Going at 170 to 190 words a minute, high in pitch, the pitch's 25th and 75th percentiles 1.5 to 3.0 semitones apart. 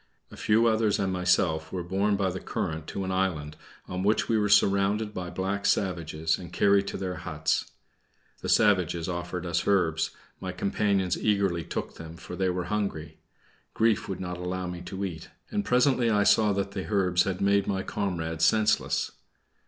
No: average, 180 wpm; very low, 95 Hz; narrow, 2.5 semitones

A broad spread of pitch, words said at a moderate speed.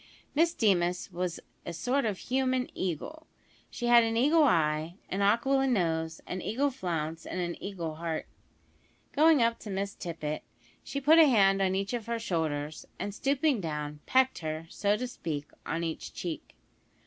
Yes: wide, 7.4 semitones; average, 170 wpm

